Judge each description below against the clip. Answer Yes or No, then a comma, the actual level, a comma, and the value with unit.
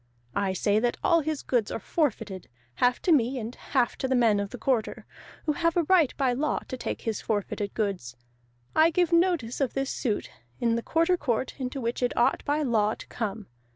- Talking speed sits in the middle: No, fast, 210 wpm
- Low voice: No, high, 245 Hz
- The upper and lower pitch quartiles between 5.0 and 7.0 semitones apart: Yes, wide, 5.6 semitones